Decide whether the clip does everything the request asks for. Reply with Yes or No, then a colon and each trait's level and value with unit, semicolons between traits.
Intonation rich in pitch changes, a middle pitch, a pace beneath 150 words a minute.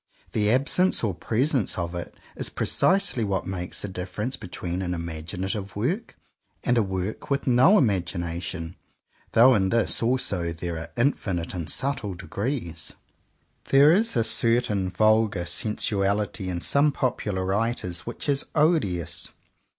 No: wide, 5.8 semitones; low, 100 Hz; slow, 135 wpm